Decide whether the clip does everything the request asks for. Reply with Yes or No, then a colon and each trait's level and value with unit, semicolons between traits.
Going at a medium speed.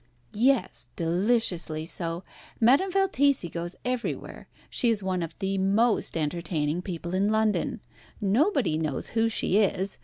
No: slow, 130 wpm